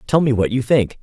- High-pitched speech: No, low, 120 Hz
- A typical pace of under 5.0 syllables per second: No, 5.7 syllables/s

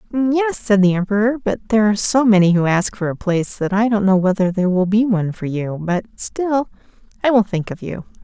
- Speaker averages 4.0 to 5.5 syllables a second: No, 6.1 syllables/s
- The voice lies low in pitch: No, high, 205 Hz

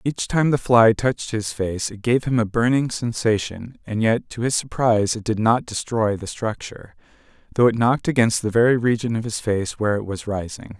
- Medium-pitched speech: No, low, 115 Hz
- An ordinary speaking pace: No, fast, 210 wpm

